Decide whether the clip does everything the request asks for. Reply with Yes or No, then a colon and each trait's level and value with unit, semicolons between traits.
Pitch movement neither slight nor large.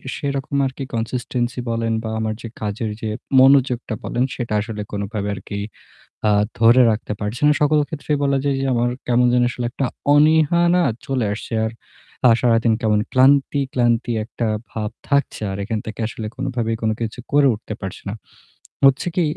Yes: average, 3.6 semitones